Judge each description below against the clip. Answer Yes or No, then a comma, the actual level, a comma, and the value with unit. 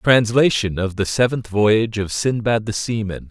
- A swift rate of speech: No, average, 180 wpm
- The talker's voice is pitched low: Yes, low, 110 Hz